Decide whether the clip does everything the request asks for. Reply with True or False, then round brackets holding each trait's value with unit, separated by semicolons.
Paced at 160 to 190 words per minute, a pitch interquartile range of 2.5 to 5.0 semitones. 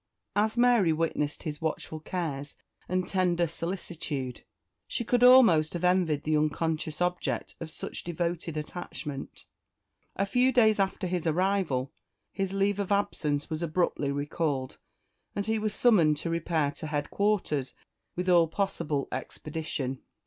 False (135 wpm; 4.3 semitones)